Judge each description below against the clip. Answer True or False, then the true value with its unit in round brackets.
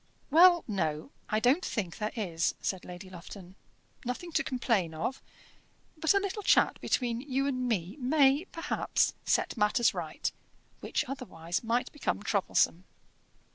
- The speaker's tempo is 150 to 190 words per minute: False (140 wpm)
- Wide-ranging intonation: True (6.9 semitones)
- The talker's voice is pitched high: True (235 Hz)